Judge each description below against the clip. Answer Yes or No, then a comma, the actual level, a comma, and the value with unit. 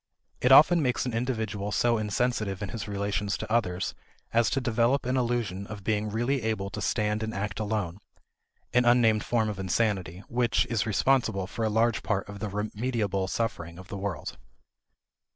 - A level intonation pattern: No, average, 3.0 semitones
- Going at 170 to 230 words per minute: Yes, average, 175 wpm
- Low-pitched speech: Yes, low, 110 Hz